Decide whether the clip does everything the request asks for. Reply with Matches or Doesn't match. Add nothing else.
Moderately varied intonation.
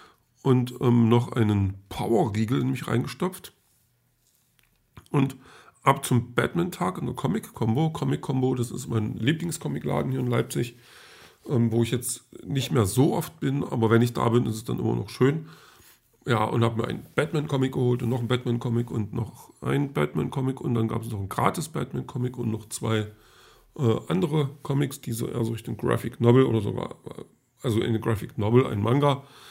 Matches